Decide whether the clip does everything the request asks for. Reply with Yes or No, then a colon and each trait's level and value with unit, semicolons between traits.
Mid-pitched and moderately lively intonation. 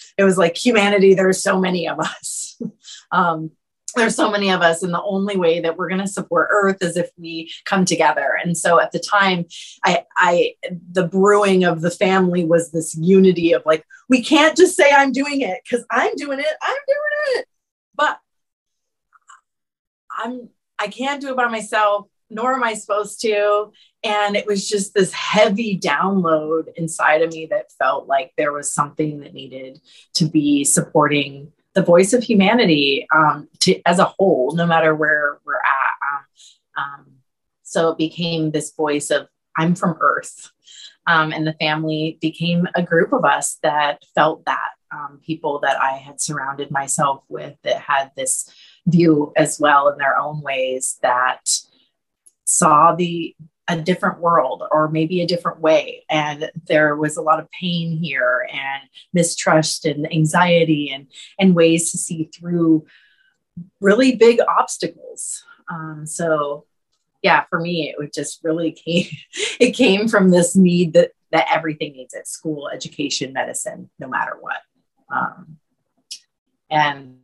Yes: medium, 170 Hz; average, 4.4 semitones